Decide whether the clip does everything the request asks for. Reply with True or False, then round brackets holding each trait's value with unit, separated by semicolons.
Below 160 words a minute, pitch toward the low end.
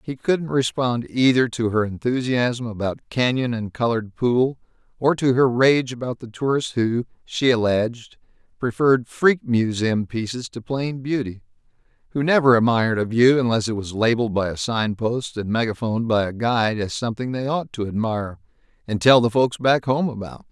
False (165 wpm; 120 Hz)